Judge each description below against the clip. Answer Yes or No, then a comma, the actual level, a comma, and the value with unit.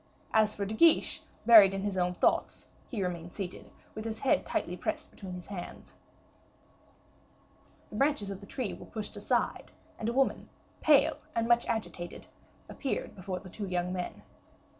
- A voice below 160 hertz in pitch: No, high, 205 Hz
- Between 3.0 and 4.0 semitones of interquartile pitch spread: Yes, average, 3.7 semitones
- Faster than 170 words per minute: No, average, 165 wpm